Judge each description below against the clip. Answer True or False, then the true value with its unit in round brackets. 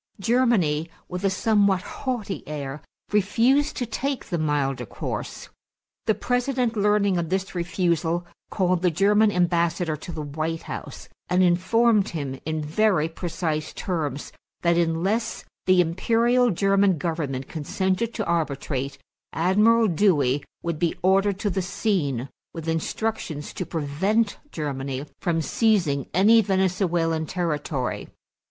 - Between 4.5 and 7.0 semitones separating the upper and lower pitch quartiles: True (4.8 semitones)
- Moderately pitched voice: True (180 Hz)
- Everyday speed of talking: False (125 wpm)